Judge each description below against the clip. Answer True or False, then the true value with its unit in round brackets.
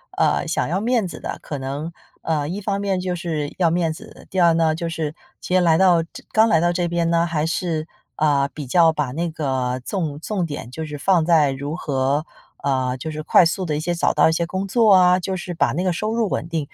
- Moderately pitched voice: True (165 Hz)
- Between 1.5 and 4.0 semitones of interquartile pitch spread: True (3.2 semitones)